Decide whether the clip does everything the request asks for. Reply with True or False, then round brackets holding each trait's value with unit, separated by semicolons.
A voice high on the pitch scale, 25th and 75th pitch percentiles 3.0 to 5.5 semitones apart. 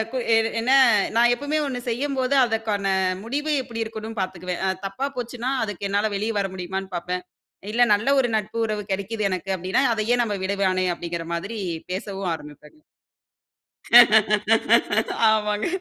True (210 Hz; 3.6 semitones)